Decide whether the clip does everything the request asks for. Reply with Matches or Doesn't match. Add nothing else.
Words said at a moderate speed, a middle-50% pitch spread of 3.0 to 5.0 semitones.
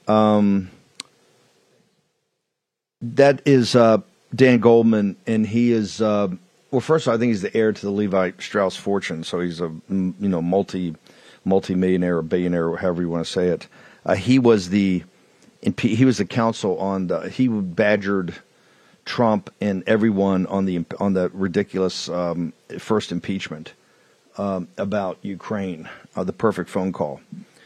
Matches